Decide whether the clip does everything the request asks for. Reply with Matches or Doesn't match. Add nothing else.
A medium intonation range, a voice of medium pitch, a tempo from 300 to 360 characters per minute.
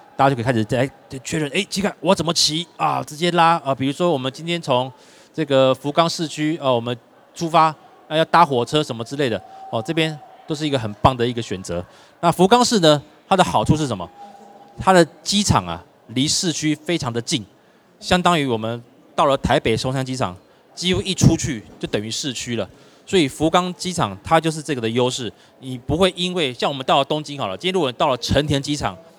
Matches